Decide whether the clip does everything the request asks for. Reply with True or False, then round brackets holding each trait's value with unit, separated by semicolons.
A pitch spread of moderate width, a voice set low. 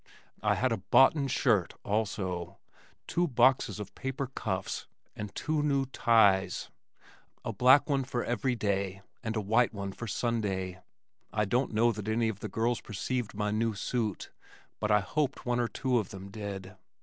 True (3.8 semitones; 110 Hz)